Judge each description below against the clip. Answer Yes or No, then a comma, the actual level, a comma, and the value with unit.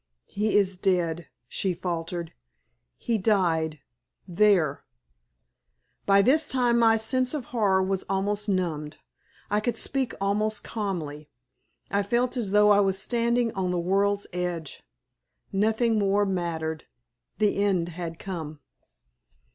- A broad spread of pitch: No, average, 3.8 semitones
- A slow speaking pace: Yes, slow, 125 wpm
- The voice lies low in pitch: No, high, 195 Hz